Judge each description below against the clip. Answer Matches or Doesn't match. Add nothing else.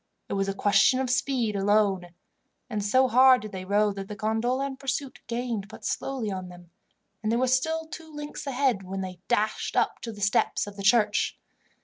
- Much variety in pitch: Doesn't match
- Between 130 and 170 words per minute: Doesn't match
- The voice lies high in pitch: Matches